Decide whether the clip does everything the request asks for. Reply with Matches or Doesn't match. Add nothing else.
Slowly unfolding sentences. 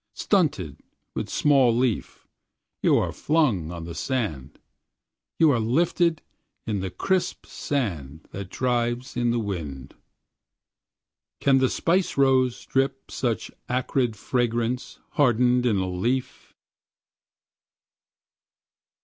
Matches